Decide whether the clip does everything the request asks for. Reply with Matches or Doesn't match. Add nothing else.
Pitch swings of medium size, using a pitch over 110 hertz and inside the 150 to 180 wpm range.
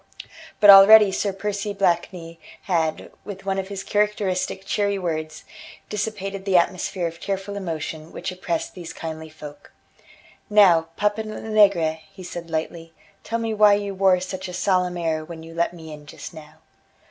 Matches